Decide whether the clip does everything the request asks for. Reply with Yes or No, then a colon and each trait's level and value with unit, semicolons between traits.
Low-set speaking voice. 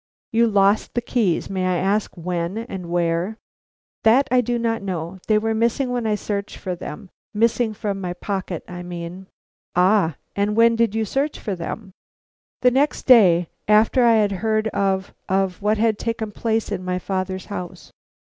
No: high, 205 Hz